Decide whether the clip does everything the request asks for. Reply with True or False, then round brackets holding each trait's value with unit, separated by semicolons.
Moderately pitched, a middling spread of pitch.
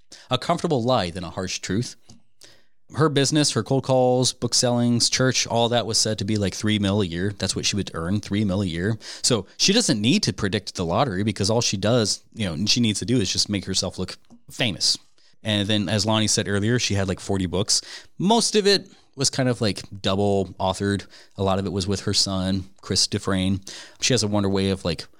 False (105 Hz; 3.9 semitones)